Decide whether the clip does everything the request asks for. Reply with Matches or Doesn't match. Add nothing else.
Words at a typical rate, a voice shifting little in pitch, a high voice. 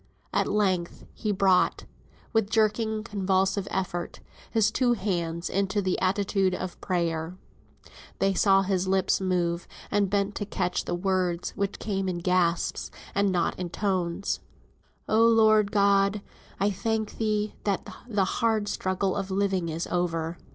Matches